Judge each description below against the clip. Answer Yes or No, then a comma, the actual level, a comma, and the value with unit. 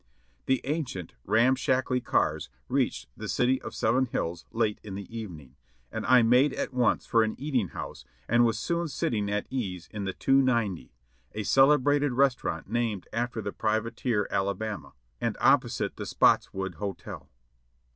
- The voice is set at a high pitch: No, low, 115 Hz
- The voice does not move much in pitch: No, average, 4.3 semitones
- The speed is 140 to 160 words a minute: Yes, average, 155 wpm